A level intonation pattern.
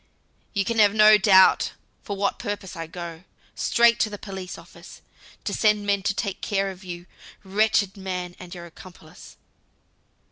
Yes: narrow, 2.3 semitones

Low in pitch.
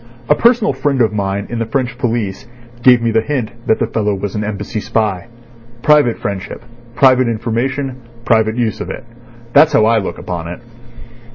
Yes: low, 115 Hz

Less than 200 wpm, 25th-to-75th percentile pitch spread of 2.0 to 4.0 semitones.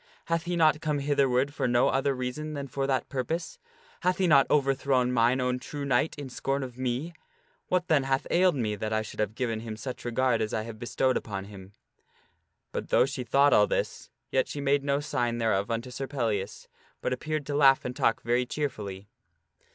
No: fast, 205 wpm; average, 3.5 semitones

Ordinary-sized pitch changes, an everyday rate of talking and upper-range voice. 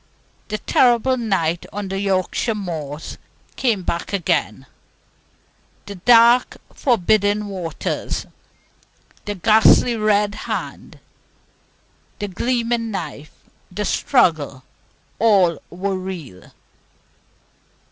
No: average, 4.2 semitones; slow, 85 wpm; high, 200 Hz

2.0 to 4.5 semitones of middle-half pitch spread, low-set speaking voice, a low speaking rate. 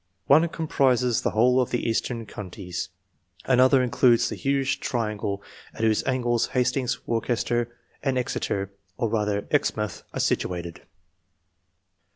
Yes: average, 3.1 semitones; low, 120 Hz; slow, 125 wpm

